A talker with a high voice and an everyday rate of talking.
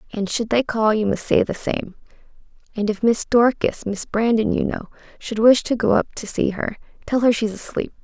No: high, 220 Hz; fast, 210 wpm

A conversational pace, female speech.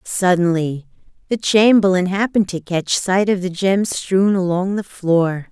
Yes: average, 150 wpm; female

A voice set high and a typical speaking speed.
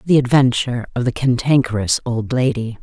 No: low, 125 Hz; average, 150 wpm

